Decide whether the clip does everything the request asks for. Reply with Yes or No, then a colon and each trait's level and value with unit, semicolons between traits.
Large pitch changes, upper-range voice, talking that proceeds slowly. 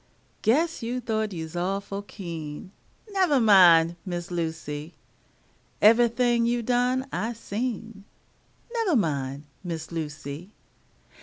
Yes: wide, 6.4 semitones; high, 200 Hz; slow, 100 wpm